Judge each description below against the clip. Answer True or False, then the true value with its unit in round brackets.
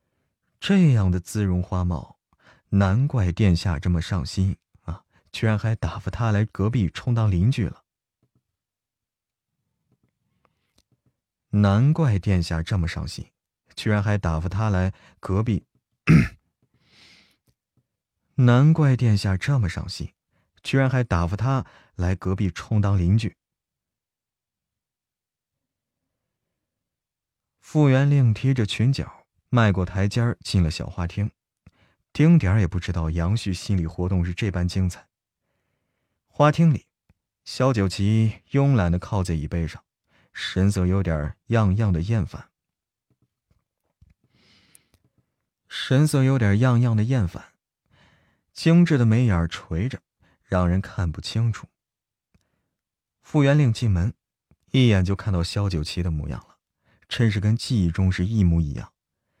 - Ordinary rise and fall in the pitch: True (4.7 semitones)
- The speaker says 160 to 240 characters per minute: True (180 characters per minute)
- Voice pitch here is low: True (100 Hz)